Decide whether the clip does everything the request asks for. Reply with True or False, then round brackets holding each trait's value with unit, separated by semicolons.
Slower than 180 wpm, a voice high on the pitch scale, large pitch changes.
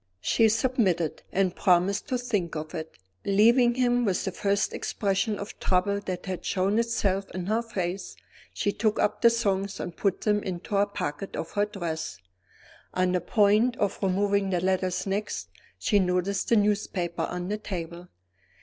False (165 wpm; 195 Hz; 2.6 semitones)